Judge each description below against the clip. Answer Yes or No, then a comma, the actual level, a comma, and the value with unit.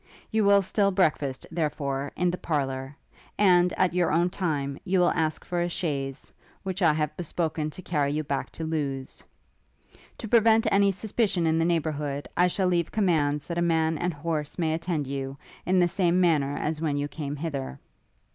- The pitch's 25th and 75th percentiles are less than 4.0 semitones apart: Yes, average, 3.6 semitones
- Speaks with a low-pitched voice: No, medium, 160 Hz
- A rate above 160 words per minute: Yes, average, 185 wpm